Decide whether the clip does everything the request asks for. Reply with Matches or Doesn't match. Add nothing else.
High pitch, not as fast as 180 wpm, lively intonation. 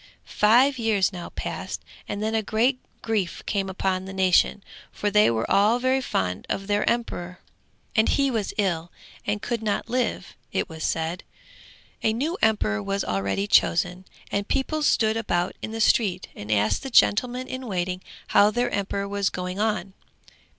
Doesn't match